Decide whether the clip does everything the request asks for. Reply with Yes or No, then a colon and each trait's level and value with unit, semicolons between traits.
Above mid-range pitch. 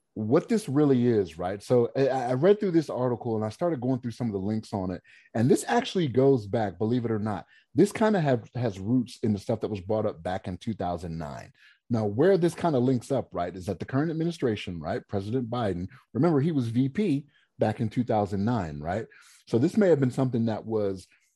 No: low, 120 Hz